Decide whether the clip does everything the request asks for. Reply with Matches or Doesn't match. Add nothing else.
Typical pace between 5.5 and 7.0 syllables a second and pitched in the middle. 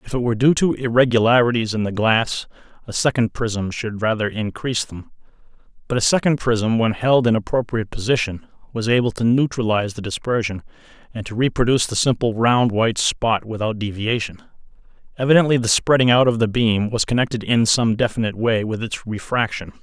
Doesn't match